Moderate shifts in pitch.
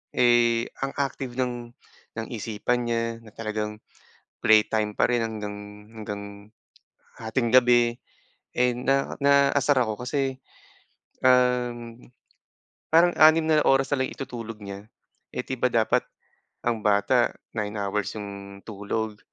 Yes: average, 3.0 semitones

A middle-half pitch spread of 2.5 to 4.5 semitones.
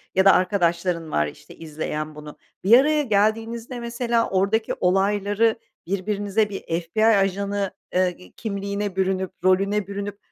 Yes: average, 2.8 semitones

